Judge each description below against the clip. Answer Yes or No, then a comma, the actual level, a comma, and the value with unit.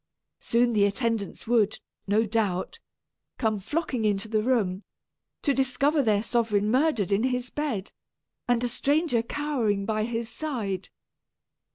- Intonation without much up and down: No, average, 3.6 semitones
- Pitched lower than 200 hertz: No, high, 230 Hz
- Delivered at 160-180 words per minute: No, slow, 135 wpm